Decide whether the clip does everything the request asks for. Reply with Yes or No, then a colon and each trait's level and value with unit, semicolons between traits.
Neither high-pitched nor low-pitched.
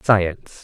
No: very low, 95 Hz